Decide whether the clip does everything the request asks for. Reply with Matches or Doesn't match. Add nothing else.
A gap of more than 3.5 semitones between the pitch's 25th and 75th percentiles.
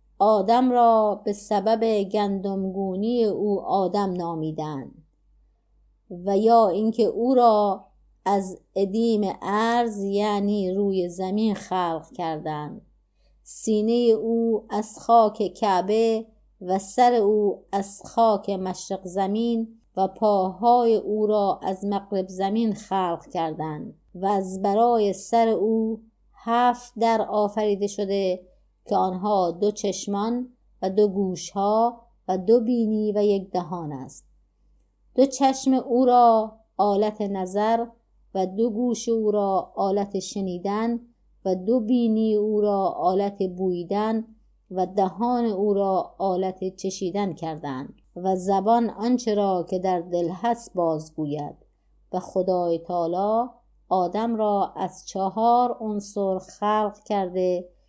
Doesn't match